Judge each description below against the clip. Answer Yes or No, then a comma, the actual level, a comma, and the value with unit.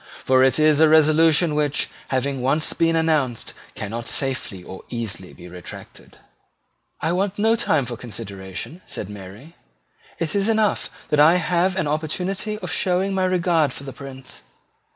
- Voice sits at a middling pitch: Yes, medium, 150 Hz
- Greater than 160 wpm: No, average, 155 wpm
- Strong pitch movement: Yes, wide, 6.0 semitones